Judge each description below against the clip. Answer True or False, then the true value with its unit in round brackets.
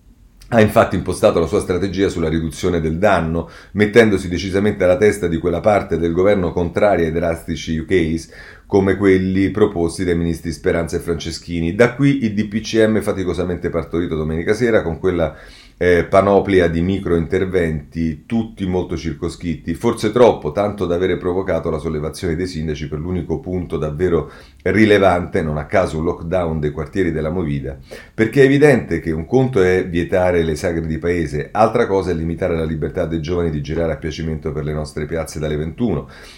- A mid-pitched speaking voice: False (85 Hz)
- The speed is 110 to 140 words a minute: False (170 wpm)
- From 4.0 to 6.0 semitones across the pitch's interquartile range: False (3.1 semitones)